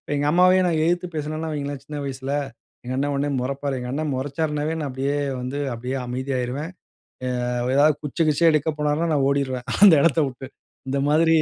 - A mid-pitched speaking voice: Yes, medium, 145 Hz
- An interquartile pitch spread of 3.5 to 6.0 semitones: No, average, 2.7 semitones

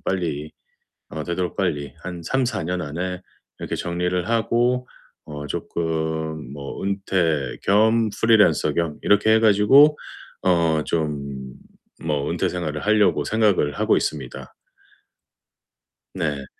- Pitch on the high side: No, very low, 85 Hz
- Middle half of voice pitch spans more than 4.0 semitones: Yes, average, 5.3 semitones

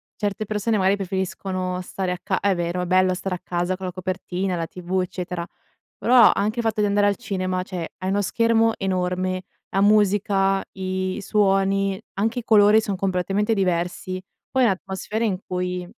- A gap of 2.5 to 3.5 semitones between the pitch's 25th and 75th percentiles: No, narrow, 1.9 semitones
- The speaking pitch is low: No, high, 190 Hz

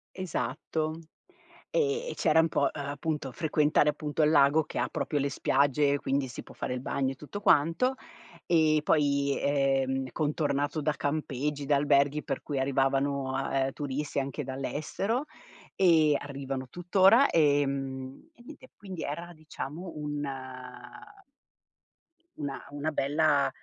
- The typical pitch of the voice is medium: Yes, medium, 145 Hz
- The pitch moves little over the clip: Yes, narrow, 2.3 semitones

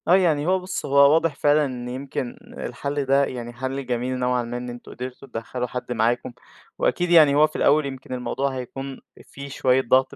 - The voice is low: Yes, low, 130 Hz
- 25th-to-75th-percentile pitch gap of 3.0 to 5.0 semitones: No, narrow, 2.4 semitones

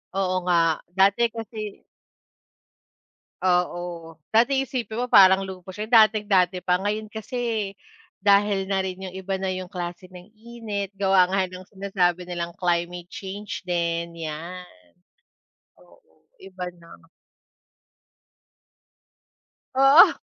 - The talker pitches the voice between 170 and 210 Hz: Yes, high, 190 Hz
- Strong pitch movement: No, average, 2.9 semitones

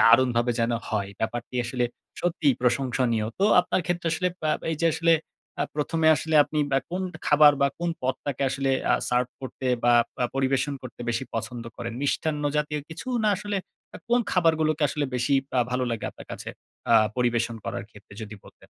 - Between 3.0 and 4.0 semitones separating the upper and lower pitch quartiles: No, average, 4.6 semitones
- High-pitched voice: No, low, 135 Hz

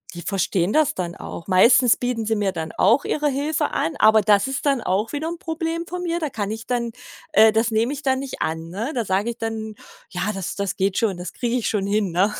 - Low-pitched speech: No, high, 220 Hz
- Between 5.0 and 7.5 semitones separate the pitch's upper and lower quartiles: Yes, average, 5.3 semitones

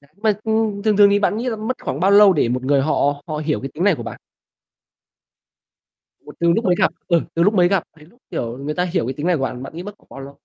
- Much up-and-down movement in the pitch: Yes, wide, 6.1 semitones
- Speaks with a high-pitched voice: No, medium, 170 Hz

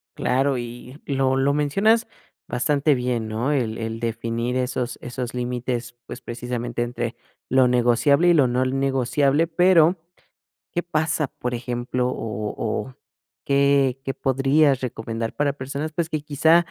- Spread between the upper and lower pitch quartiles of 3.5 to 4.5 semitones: No, average, 3.0 semitones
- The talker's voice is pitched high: No, low, 130 Hz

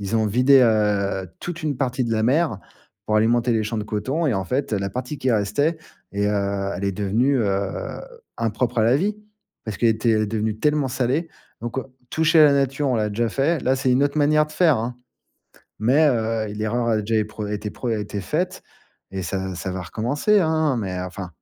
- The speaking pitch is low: Yes, low, 115 Hz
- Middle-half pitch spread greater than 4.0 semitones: Yes, average, 5.0 semitones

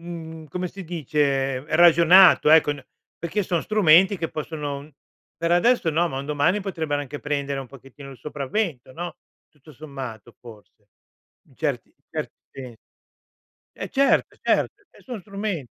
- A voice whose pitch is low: No, medium, 155 Hz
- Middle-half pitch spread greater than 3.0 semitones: Yes, average, 4.0 semitones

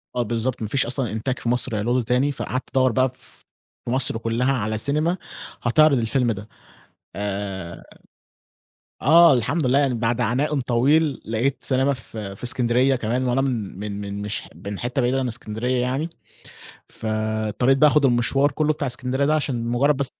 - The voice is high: No, low, 125 Hz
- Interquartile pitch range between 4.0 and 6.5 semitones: No, average, 3.3 semitones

